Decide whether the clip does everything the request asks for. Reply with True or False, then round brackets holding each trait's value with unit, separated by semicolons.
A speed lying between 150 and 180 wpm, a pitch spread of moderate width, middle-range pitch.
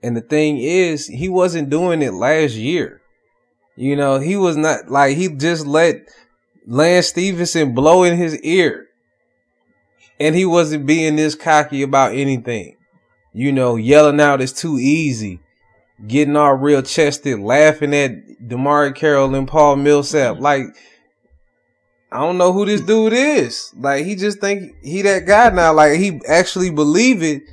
True (155 wpm; 3.8 semitones; 150 Hz)